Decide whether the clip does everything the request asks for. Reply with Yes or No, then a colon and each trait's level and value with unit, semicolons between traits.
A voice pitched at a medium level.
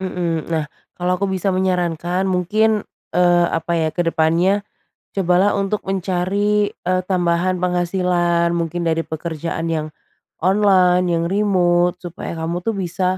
Yes: medium, 180 Hz